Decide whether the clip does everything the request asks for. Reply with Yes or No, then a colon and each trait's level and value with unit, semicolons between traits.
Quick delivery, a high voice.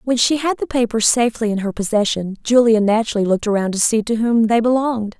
Yes: fast, 220 wpm; high, 225 Hz